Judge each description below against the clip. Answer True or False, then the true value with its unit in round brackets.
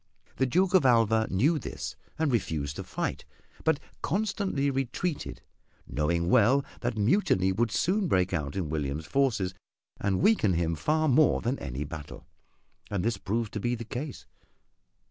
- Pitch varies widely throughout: True (7.5 semitones)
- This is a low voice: True (115 Hz)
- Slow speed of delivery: False (155 wpm)